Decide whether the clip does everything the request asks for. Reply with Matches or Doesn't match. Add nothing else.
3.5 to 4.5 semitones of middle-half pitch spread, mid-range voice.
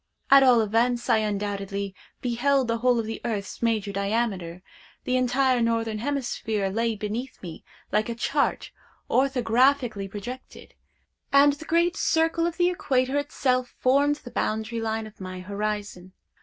Doesn't match